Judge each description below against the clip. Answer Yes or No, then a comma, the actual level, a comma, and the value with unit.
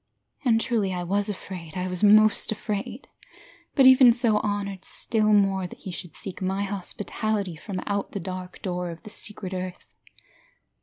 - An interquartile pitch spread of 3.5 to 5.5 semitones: No, narrow, 2.6 semitones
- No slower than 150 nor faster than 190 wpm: Yes, average, 165 wpm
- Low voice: No, high, 200 Hz